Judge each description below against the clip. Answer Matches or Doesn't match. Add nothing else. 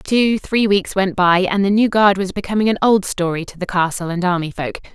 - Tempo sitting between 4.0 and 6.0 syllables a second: Matches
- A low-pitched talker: Doesn't match